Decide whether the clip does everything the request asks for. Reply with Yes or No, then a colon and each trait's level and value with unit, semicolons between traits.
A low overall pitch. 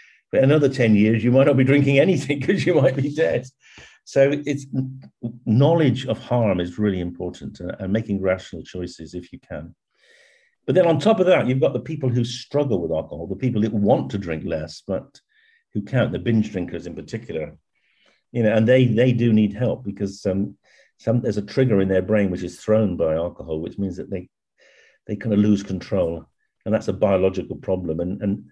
Yes: low, 110 Hz